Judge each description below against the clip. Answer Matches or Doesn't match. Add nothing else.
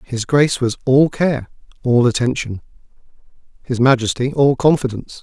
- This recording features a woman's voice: Doesn't match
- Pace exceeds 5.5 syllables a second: Doesn't match